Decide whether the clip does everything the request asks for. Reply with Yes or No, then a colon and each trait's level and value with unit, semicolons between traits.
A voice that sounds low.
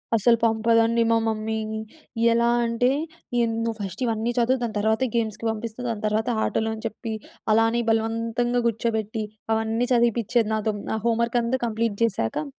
No: high, 225 Hz